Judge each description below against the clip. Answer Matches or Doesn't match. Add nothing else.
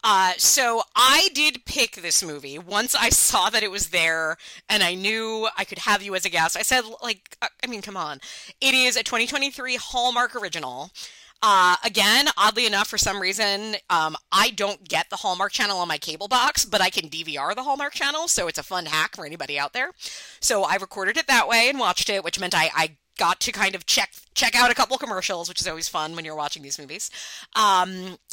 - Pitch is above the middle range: Matches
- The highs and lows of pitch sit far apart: Matches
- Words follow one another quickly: Matches